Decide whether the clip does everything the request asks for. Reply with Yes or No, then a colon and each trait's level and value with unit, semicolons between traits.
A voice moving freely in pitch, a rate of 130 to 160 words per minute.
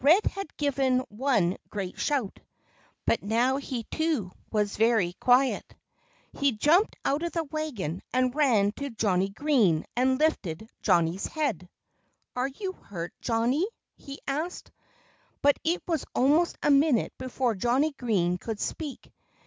Yes: wide, 6.0 semitones; average, 140 wpm